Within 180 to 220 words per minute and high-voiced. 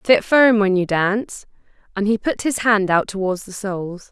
Yes: fast, 205 wpm; high, 205 Hz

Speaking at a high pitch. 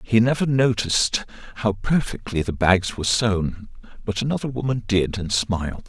No: low, 110 Hz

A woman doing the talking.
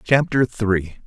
No: male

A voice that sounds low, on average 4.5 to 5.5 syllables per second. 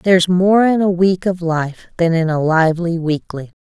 No: medium, 175 Hz; 4.7 syllables/s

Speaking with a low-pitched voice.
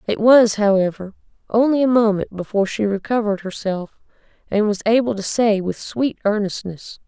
No: high, 210 Hz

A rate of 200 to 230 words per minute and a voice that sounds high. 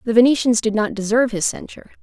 Yes: fast, 205 wpm; high, 225 Hz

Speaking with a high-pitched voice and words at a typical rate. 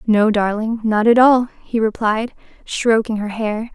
Yes: high, 220 Hz; average, 160 wpm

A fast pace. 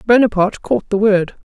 No: average, 155 wpm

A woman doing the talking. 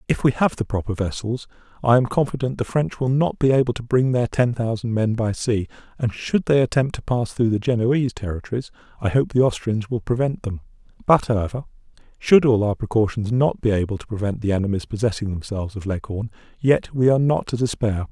No: male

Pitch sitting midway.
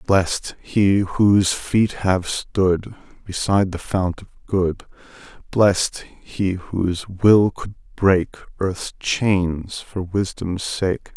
No: very low, 95 Hz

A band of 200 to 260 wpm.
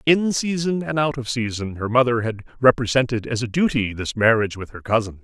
Yes: fast, 205 wpm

